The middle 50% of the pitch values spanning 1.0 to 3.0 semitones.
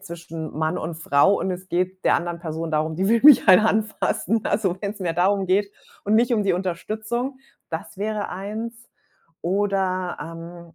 No: average, 3.7 semitones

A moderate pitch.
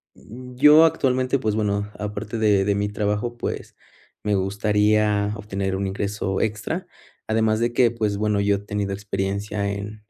No: low, 105 Hz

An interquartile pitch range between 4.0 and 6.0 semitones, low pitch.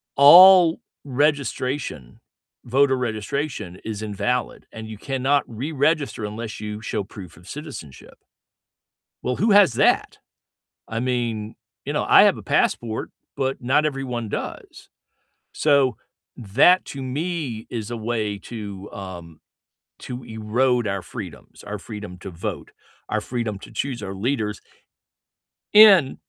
Yes: average, 4.8 semitones; low, 120 Hz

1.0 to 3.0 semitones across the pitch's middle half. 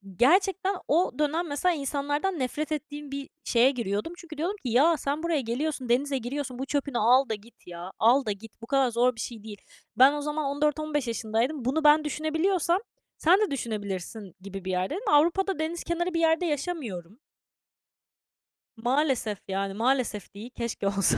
No: wide, 5.4 semitones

